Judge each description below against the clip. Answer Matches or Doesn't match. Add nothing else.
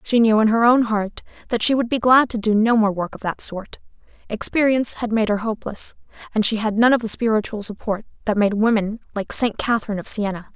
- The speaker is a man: Doesn't match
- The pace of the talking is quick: Matches